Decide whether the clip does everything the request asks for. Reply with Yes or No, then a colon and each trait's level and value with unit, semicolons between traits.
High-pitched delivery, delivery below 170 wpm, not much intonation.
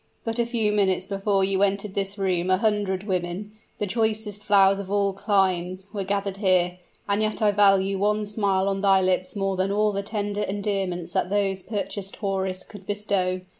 No: high, 200 Hz; average, 185 wpm; narrow, 1.5 semitones